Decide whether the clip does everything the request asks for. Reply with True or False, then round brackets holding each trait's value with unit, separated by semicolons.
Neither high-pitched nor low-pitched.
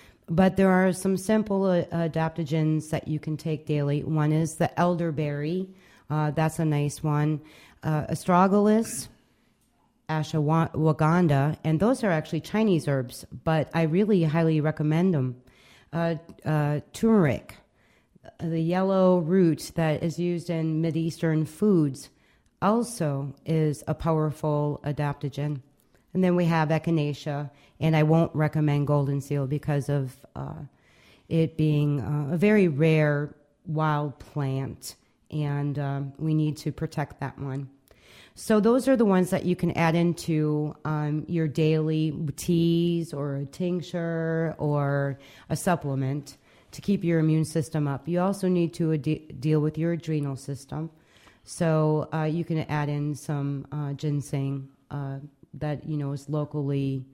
True (155 Hz)